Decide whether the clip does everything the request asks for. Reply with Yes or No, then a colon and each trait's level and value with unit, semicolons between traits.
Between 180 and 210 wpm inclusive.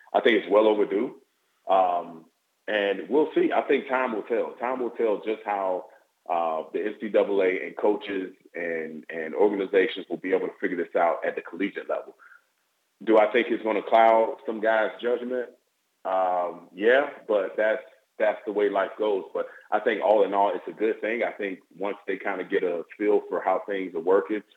Yes: average, 200 wpm